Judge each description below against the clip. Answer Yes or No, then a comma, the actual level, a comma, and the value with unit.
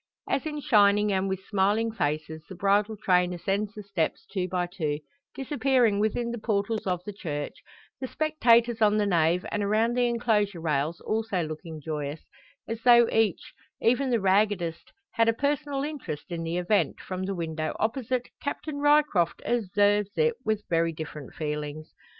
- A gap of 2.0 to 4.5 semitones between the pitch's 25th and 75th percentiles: No, average, 5.1 semitones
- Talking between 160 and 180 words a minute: Yes, average, 165 wpm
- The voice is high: Yes, high, 205 Hz